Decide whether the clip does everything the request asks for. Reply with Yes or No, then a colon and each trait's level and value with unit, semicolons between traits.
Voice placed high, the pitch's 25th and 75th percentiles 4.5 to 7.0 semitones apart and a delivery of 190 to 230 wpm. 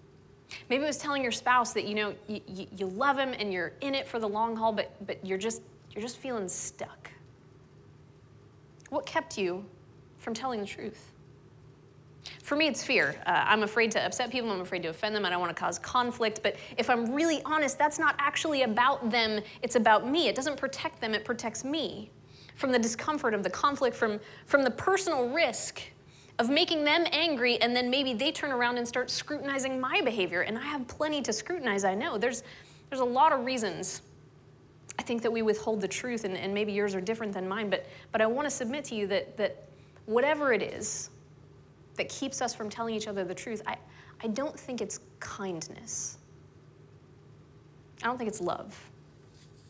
Yes: high, 230 Hz; average, 5.2 semitones; average, 200 wpm